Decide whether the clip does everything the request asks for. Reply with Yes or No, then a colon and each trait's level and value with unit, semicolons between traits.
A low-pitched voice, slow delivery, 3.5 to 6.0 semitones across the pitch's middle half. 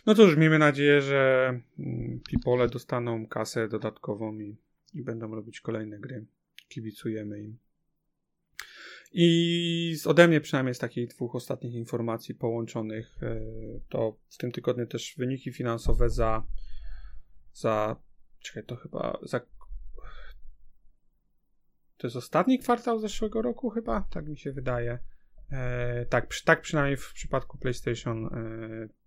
No: low, 120 Hz; average, 125 wpm; average, 4.5 semitones